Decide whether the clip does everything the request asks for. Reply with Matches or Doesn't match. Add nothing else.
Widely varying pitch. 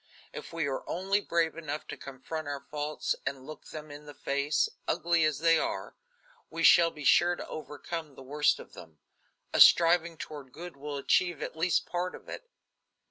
Doesn't match